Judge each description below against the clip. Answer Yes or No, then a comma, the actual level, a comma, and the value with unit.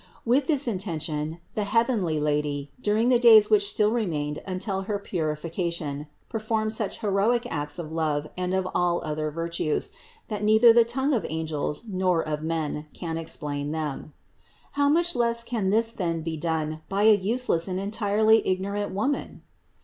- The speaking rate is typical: Yes, average, 160 wpm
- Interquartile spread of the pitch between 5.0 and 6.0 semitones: Yes, wide, 5.6 semitones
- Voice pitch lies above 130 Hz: Yes, high, 190 Hz